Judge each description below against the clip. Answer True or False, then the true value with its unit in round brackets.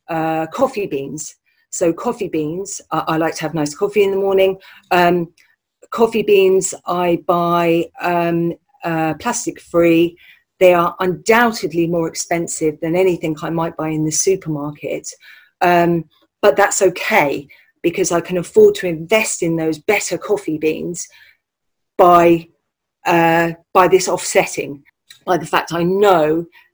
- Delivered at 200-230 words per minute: False (140 wpm)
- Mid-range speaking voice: True (175 Hz)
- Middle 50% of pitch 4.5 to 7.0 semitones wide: False (3.3 semitones)